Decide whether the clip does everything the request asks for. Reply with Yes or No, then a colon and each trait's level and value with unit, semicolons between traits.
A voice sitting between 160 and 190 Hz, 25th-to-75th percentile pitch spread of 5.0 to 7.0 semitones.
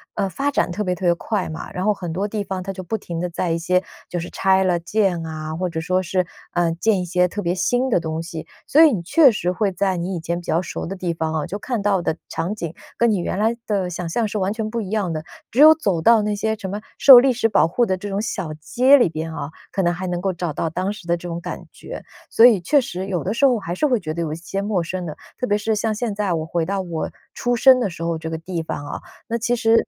No: medium, 185 Hz; average, 4.0 semitones